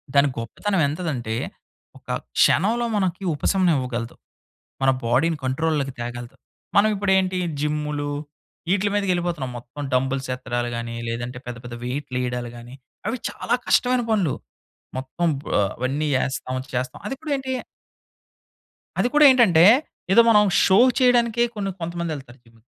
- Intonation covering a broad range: Yes, wide, 7.7 semitones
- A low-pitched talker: No, medium, 150 Hz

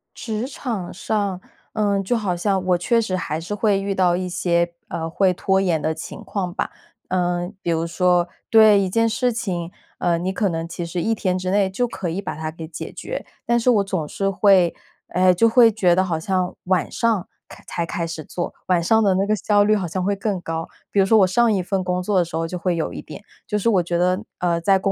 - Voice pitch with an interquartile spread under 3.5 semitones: Yes, average, 2.9 semitones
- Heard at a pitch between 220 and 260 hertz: No, medium, 185 Hz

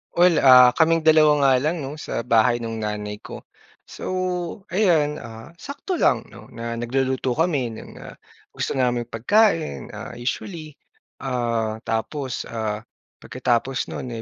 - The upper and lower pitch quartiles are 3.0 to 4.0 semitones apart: No, wide, 5.4 semitones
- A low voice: Yes, low, 130 Hz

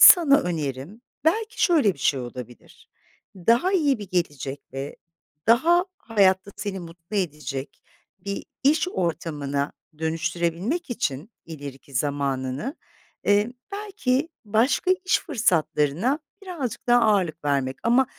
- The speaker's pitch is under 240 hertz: Yes, high, 190 Hz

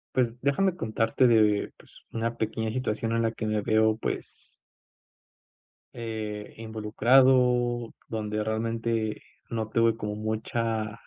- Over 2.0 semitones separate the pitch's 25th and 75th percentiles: No, narrow, 1.3 semitones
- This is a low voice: Yes, low, 115 Hz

